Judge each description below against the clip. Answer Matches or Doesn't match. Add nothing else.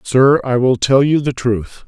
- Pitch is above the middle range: Doesn't match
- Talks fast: Matches